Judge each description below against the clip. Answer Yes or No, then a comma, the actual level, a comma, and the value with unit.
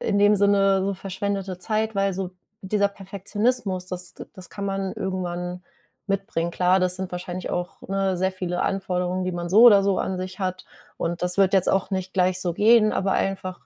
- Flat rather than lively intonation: Yes, narrow, 1.5 semitones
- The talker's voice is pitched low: No, high, 190 Hz